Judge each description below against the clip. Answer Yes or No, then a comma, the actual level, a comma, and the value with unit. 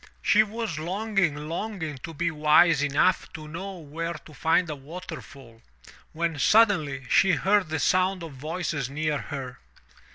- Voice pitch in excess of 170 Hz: No, medium, 160 Hz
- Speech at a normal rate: Yes, average, 150 wpm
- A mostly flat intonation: No, average, 3.8 semitones